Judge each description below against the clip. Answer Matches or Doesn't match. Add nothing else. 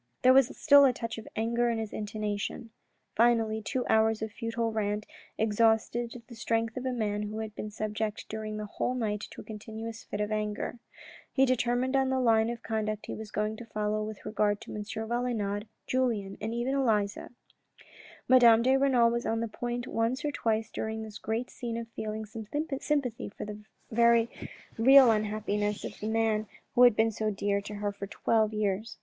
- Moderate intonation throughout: Doesn't match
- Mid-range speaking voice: Doesn't match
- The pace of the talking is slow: Doesn't match